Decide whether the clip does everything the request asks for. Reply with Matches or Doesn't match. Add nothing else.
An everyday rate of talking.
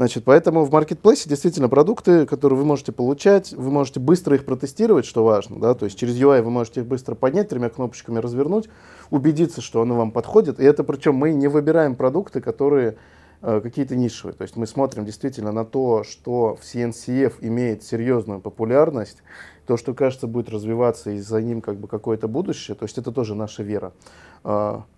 Doesn't match